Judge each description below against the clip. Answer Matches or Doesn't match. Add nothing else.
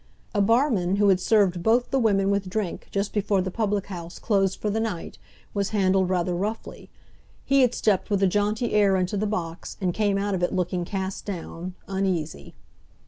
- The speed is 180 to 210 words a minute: Matches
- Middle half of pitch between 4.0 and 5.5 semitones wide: Doesn't match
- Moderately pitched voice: Doesn't match